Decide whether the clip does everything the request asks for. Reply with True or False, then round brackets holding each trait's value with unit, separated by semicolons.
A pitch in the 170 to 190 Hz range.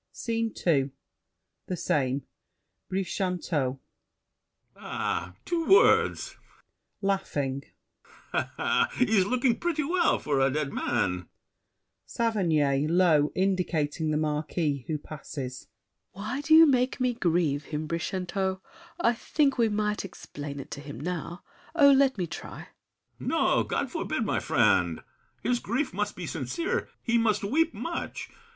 True (185 Hz)